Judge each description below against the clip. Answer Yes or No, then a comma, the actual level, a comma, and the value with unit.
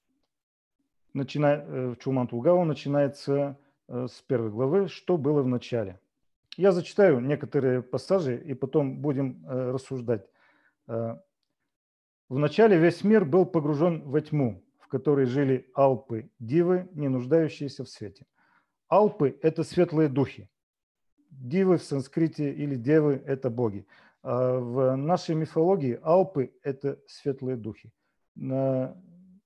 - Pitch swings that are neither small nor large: Yes, average, 4.2 semitones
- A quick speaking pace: No, average, 115 wpm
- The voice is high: No, medium, 140 Hz